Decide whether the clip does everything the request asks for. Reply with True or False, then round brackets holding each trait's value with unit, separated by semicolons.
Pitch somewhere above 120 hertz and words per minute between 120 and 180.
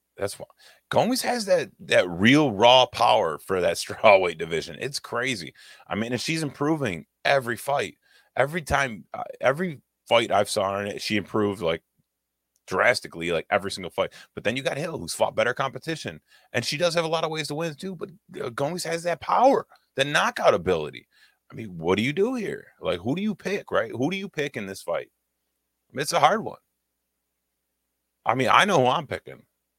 False (135 Hz; 200 wpm)